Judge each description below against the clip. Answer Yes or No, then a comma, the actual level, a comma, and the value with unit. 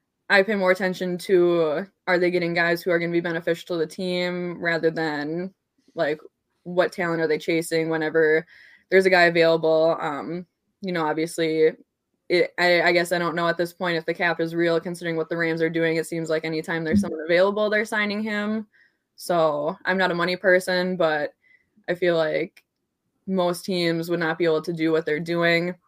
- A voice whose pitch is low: No, medium, 170 Hz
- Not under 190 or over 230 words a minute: Yes, average, 200 wpm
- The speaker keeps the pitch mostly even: Yes, narrow, 1.9 semitones